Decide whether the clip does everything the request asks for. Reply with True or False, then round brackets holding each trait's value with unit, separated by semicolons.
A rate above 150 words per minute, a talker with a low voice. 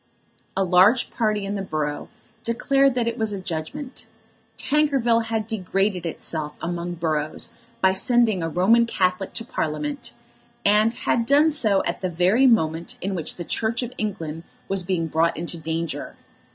False (160 wpm; 195 Hz)